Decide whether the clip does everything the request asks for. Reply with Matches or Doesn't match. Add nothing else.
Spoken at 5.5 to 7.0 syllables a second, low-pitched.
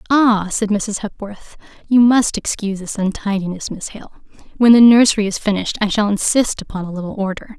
Doesn't match